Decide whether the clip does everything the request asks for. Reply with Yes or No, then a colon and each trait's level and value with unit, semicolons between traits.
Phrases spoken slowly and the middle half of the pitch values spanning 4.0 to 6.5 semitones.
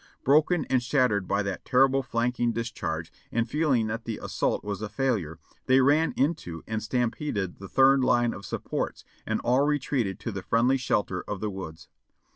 No: average, 180 wpm; average, 4.7 semitones